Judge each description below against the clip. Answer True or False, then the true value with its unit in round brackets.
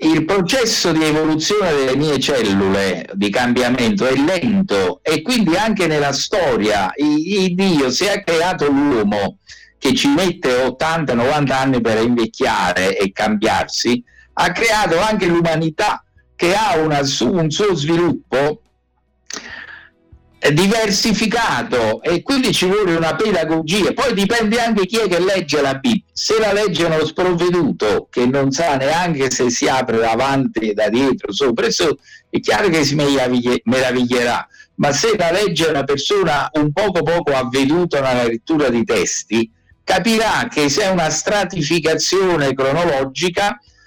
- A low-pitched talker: False (160 Hz)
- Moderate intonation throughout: False (7.1 semitones)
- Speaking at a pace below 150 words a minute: True (135 wpm)